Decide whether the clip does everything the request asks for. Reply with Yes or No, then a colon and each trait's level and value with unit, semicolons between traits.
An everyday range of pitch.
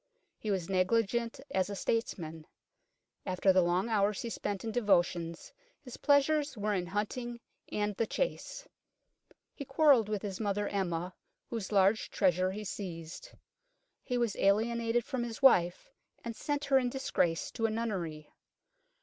Yes: average, 4.2 semitones